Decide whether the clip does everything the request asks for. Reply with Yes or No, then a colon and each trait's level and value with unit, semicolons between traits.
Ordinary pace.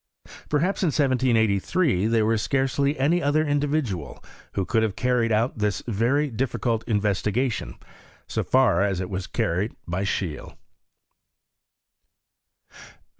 No: slow, 125 wpm